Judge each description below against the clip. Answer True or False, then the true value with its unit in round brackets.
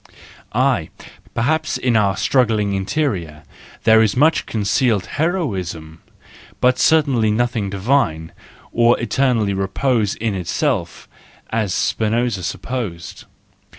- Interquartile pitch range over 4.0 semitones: True (4.6 semitones)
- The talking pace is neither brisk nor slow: False (100 wpm)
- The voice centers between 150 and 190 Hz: False (110 Hz)